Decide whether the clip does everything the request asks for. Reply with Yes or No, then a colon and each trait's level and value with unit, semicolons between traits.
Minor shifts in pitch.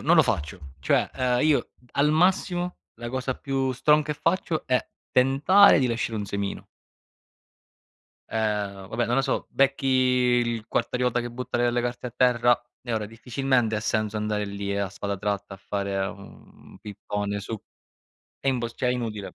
No: average, 4.0 semitones